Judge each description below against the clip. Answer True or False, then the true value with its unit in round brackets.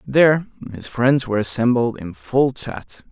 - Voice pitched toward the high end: False (125 Hz)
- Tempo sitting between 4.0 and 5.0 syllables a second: True (4.5 syllables/s)